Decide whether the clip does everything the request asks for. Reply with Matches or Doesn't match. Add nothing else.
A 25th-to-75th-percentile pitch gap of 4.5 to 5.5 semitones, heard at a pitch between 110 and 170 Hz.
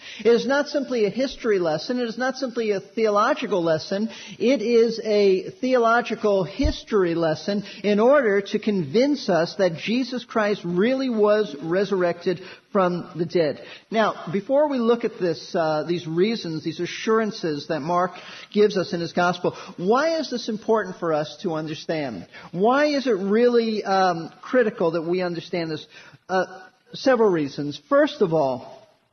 Doesn't match